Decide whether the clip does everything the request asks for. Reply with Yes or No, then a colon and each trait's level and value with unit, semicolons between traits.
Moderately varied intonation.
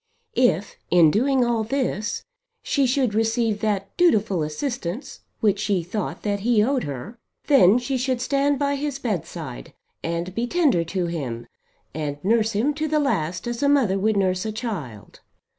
No: wide, 6.0 semitones